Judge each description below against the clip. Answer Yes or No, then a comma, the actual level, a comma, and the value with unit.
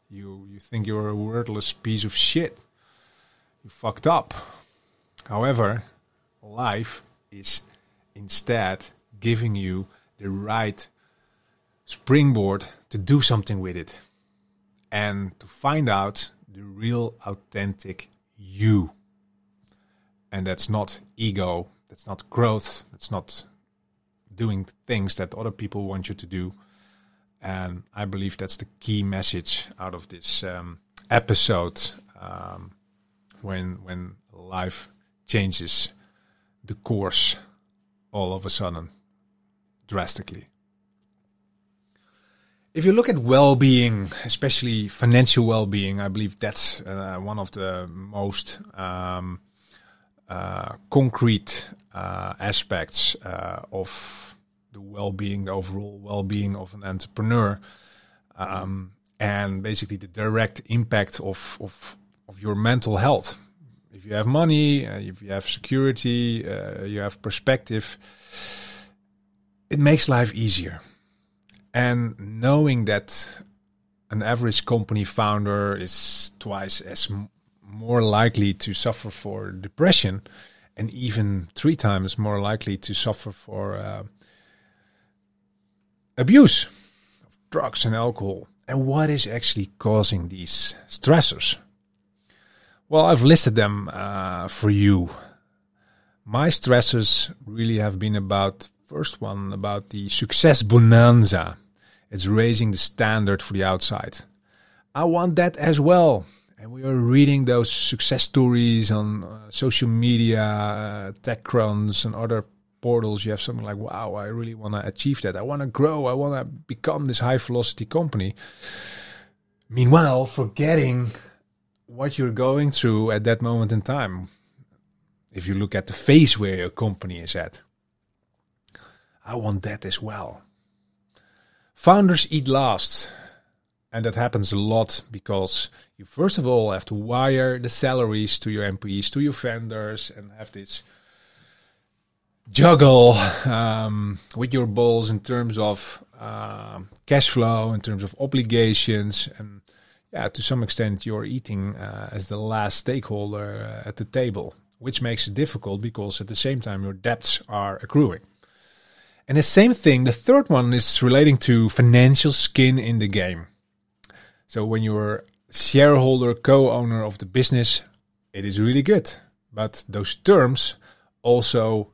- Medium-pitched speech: No, low, 105 Hz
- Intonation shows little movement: No, average, 3.3 semitones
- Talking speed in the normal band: No, slow, 130 wpm